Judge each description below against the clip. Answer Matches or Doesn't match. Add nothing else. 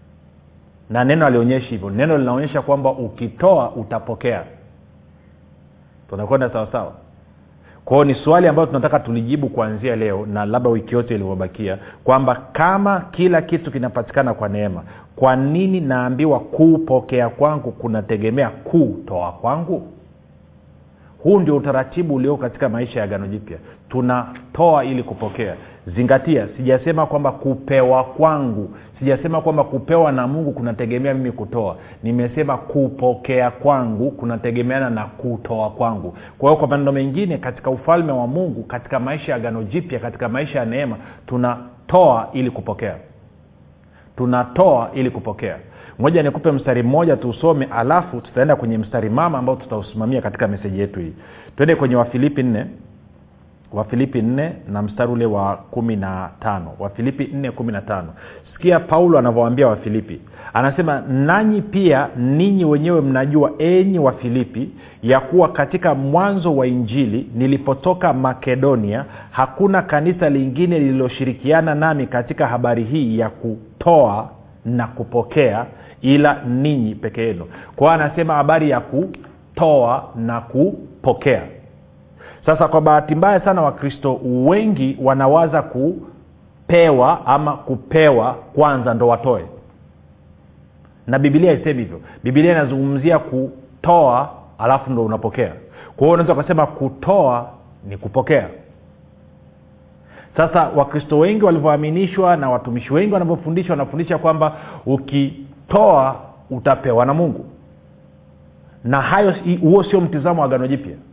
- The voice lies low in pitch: Matches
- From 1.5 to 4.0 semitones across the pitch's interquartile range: Doesn't match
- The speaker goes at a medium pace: Matches